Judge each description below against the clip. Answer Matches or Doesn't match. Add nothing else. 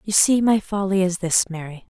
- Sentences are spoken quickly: Matches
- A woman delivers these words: Matches